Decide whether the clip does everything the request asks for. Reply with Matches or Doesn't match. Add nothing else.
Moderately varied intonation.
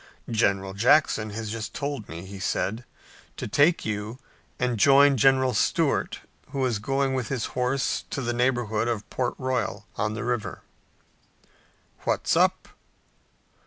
Matches